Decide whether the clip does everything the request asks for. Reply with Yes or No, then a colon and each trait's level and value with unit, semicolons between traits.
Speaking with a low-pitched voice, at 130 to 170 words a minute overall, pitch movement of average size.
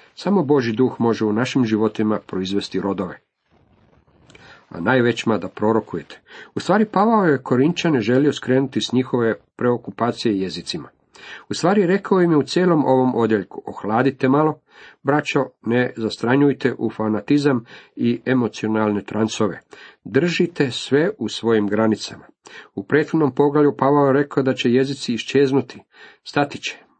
Yes: low, 130 Hz; average, 135 wpm; average, 4.7 semitones